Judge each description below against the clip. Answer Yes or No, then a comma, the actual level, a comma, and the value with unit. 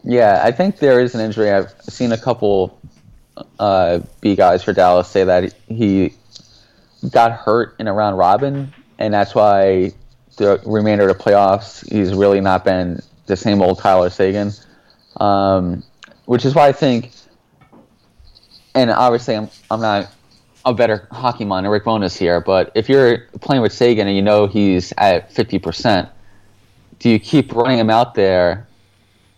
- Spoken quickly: No, average, 165 wpm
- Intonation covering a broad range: No, average, 3.5 semitones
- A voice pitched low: Yes, low, 105 Hz